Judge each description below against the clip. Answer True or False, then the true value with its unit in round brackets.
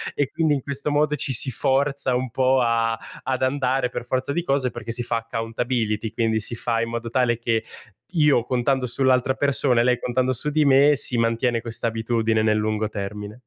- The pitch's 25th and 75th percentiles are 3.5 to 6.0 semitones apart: False (2.6 semitones)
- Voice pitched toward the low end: True (125 Hz)